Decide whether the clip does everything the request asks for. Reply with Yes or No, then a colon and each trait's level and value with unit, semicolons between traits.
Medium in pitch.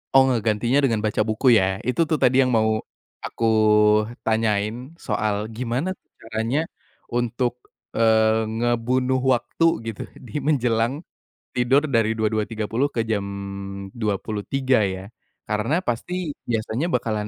No: low, 115 Hz